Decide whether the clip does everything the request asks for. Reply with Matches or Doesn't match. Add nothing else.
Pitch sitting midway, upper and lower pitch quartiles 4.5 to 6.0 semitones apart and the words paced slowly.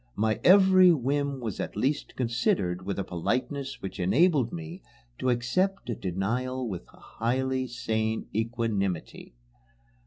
Doesn't match